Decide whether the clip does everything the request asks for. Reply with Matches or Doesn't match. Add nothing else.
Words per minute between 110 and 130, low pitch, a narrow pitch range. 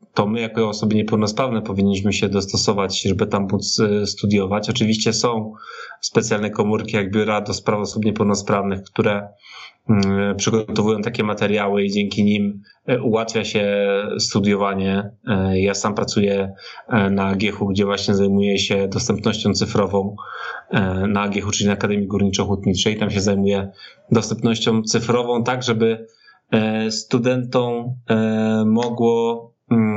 Matches